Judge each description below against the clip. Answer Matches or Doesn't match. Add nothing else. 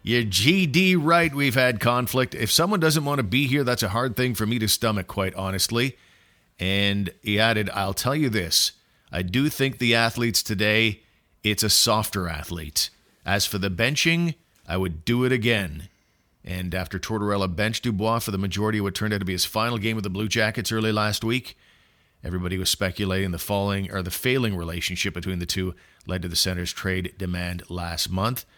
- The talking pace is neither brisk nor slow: Matches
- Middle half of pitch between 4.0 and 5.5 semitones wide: Matches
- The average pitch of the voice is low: Matches